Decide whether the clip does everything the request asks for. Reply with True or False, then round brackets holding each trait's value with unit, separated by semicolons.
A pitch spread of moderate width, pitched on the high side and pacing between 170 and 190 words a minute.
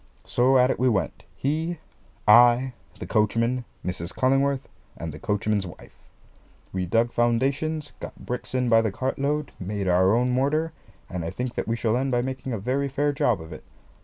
False (4.2 semitones; 120 Hz; 185 wpm)